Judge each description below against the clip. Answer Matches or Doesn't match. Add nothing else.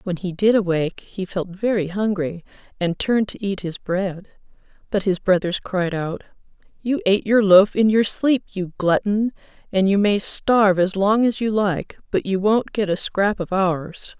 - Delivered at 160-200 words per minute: Matches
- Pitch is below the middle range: Doesn't match